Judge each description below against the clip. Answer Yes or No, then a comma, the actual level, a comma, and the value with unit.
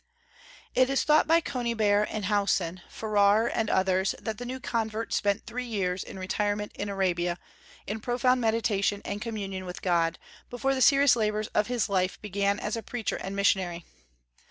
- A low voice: No, high, 210 Hz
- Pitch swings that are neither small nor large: Yes, average, 3.3 semitones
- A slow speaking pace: No, average, 170 wpm